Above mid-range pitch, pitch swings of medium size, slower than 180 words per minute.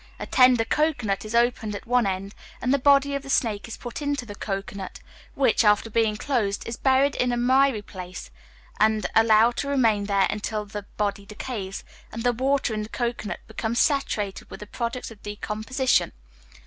No: high, 225 Hz; average, 3.5 semitones; average, 185 wpm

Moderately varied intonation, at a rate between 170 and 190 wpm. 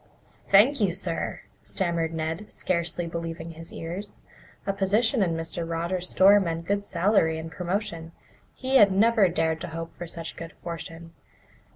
No: average, 3.1 semitones; average, 155 wpm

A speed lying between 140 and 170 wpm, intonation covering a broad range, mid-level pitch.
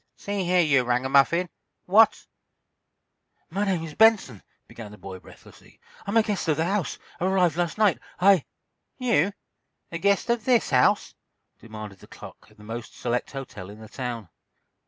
Yes: average, 155 wpm; wide, 8.9 semitones; medium, 165 Hz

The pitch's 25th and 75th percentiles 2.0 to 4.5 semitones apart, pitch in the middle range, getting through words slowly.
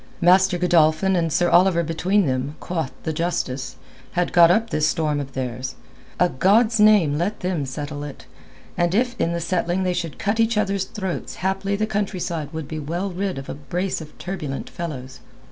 No: average, 3.9 semitones; medium, 175 Hz; average, 185 wpm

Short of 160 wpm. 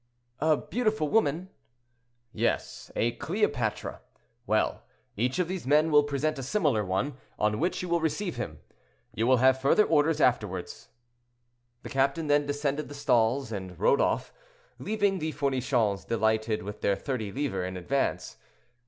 Yes: average, 150 wpm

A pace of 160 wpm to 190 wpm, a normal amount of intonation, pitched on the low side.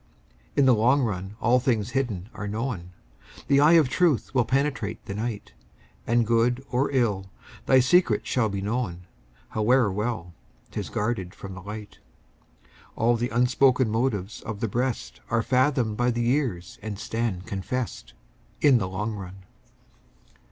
No: average, 150 wpm; average, 3.8 semitones; low, 115 Hz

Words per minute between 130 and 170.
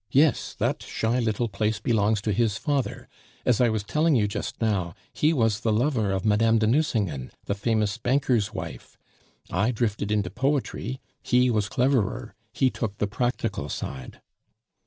Yes: average, 160 wpm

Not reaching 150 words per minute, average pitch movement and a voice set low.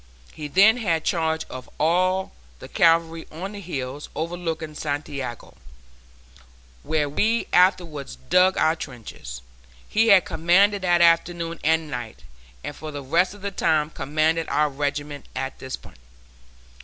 No: average, 140 wpm; average, 3.5 semitones; medium, 160 Hz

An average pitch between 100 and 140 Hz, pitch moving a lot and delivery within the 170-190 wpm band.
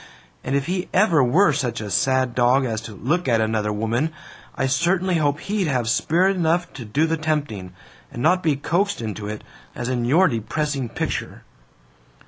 Yes: low, 135 Hz; wide, 6.3 semitones; average, 180 wpm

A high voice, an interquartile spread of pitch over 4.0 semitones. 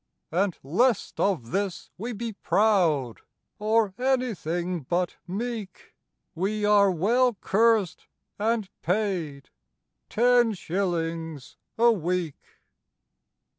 Yes: high, 195 Hz; average, 4.6 semitones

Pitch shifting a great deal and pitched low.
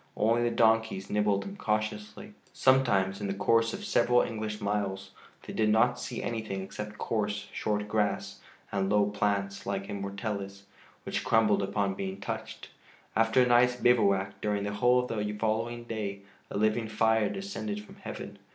No: narrow, 2.6 semitones; low, 105 Hz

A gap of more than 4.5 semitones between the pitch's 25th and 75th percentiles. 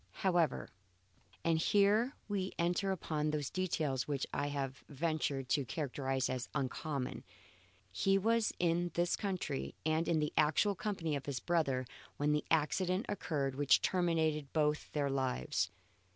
No: average, 4.1 semitones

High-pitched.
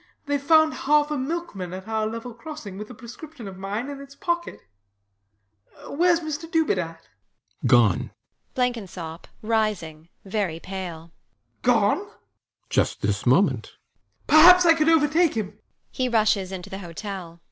Yes: high, 225 Hz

